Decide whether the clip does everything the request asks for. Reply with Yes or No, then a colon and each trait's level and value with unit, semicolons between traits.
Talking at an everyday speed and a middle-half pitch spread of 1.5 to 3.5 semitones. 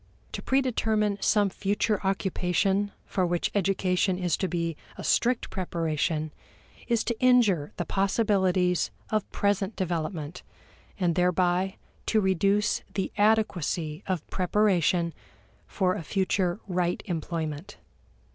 No: slow, 115 wpm; average, 2.8 semitones